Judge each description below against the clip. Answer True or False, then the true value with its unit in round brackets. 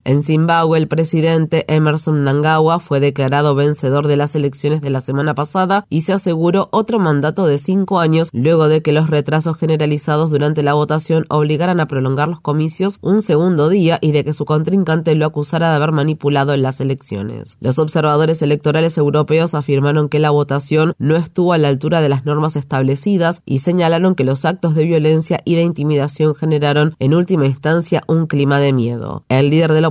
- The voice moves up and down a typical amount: False (2.1 semitones)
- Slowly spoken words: False (185 wpm)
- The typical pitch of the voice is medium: True (155 Hz)